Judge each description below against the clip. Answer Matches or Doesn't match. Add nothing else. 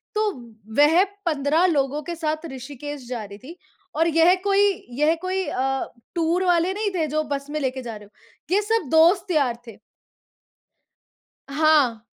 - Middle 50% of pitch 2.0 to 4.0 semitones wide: Doesn't match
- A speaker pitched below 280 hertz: Doesn't match